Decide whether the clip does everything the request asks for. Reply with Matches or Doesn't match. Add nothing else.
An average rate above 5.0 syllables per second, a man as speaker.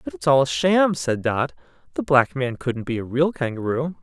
Doesn't match